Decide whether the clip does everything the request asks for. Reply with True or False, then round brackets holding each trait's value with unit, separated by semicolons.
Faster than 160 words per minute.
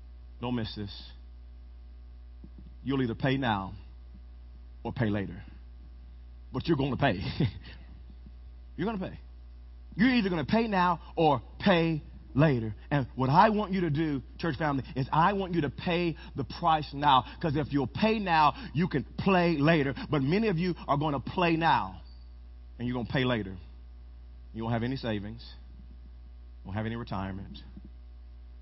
True (170 wpm)